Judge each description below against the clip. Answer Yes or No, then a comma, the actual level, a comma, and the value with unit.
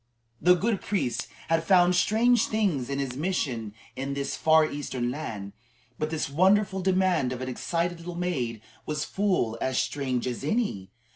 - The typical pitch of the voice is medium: Yes, medium, 155 Hz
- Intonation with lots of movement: Yes, wide, 6.3 semitones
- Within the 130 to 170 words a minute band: Yes, average, 165 wpm